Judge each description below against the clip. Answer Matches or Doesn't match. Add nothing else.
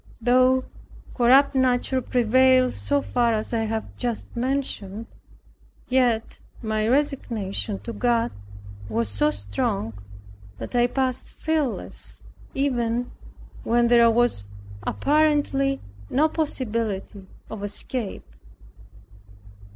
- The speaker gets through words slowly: Matches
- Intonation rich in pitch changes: Doesn't match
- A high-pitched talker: Matches